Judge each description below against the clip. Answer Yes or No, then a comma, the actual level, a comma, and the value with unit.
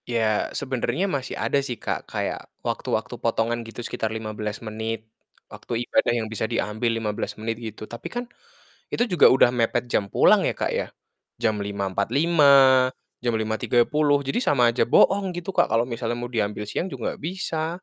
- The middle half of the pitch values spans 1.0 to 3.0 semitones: No, average, 4.1 semitones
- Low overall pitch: Yes, low, 120 Hz